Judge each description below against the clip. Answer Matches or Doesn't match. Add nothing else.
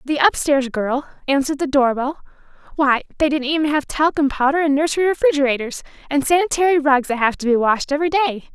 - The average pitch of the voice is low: Doesn't match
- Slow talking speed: Doesn't match